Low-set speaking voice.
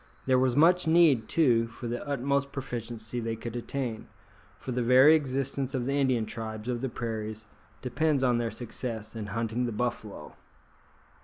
Yes: low, 125 Hz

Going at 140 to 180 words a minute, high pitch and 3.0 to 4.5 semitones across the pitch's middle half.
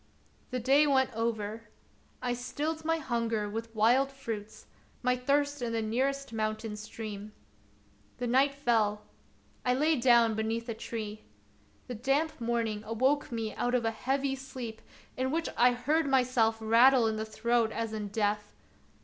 Yes: average, 155 wpm; high, 235 Hz; average, 3.3 semitones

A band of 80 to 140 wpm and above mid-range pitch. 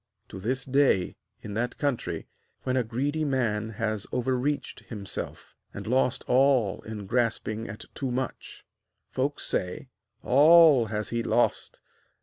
No: slow, 135 wpm; low, 125 Hz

